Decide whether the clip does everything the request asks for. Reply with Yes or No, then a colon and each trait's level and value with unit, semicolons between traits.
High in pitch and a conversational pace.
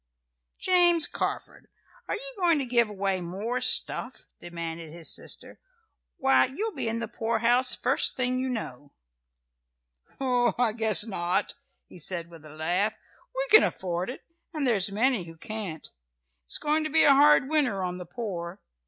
Yes: high, 225 Hz; average, 160 wpm